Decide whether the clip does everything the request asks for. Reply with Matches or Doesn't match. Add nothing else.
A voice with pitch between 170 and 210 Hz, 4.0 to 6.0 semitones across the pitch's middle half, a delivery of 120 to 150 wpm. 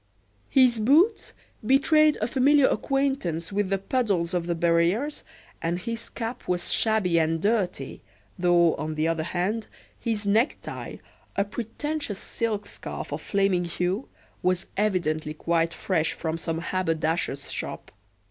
Matches